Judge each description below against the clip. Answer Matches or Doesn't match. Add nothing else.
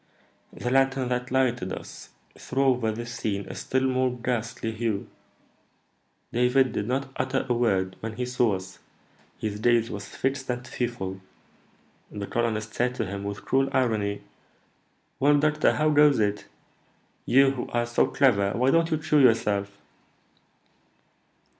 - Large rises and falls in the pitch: Doesn't match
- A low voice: Matches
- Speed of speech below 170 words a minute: Matches